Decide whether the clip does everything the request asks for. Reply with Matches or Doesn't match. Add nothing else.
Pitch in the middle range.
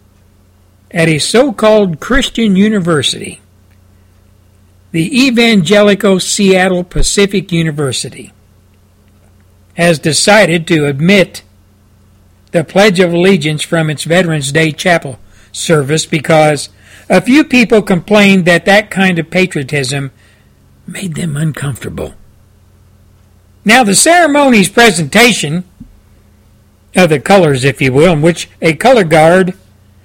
Matches